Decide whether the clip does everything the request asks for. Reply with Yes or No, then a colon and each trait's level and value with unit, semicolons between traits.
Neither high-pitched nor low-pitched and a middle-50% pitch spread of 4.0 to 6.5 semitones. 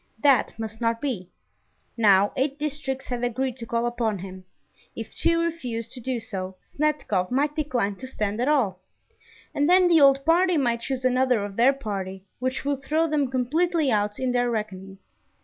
No: very high, 250 Hz; average, 4.7 semitones